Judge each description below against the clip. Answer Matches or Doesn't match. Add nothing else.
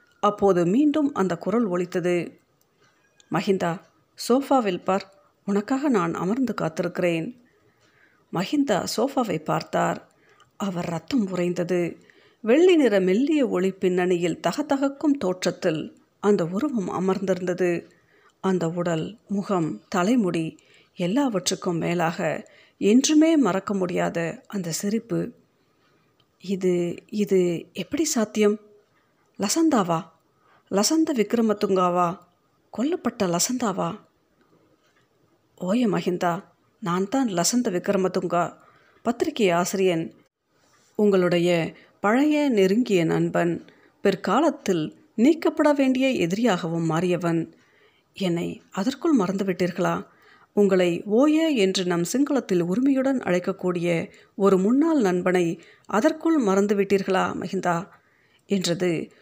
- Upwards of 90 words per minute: Doesn't match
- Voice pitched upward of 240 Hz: Doesn't match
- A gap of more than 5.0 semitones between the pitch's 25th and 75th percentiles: Matches